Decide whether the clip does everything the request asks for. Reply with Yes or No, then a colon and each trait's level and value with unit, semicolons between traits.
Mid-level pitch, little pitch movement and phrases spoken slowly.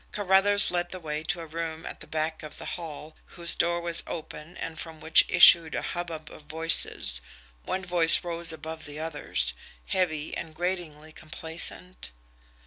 No: medium, 165 Hz; narrow, 1.9 semitones; average, 165 wpm